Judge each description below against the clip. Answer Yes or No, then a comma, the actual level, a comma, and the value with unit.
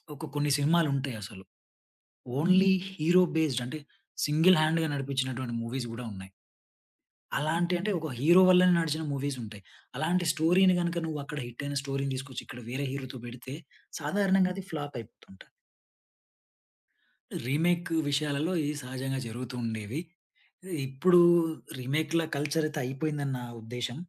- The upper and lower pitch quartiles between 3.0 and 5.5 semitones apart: Yes, average, 4.1 semitones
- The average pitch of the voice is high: No, medium, 145 Hz